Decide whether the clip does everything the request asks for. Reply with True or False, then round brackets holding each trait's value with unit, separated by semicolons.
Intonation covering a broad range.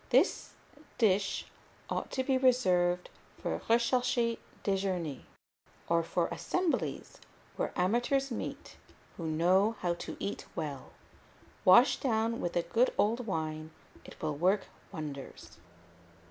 True (5.8 semitones)